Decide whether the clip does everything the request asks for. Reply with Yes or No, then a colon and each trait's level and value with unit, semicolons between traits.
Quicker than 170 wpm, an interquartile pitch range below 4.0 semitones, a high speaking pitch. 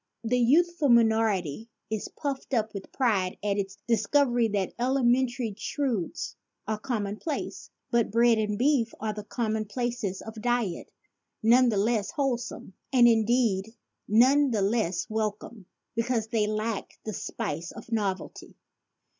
No: average, 145 wpm; average, 2.7 semitones; high, 225 Hz